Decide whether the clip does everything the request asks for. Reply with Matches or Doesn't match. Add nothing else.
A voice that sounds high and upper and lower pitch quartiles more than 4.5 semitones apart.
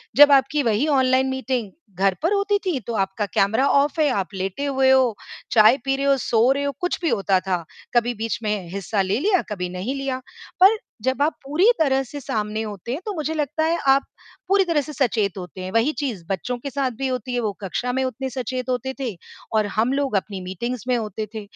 Matches